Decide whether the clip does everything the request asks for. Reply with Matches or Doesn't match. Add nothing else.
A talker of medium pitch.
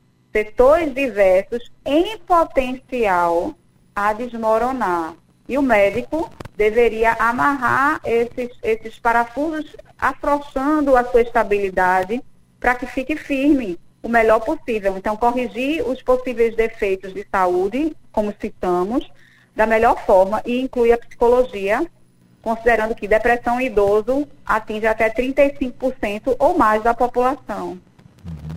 Doesn't match